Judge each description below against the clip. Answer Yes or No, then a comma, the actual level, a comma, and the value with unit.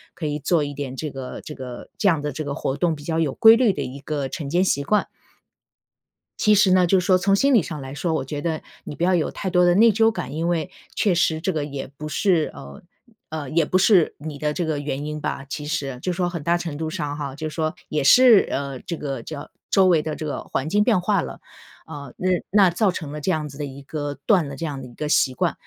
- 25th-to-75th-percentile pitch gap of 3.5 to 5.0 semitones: Yes, average, 4.0 semitones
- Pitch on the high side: No, medium, 155 Hz